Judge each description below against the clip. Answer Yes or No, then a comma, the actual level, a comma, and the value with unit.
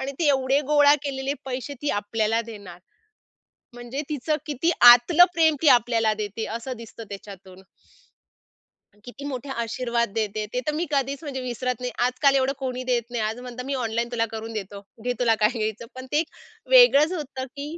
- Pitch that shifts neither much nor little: Yes, average, 3.6 semitones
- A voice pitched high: Yes, very high, 250 Hz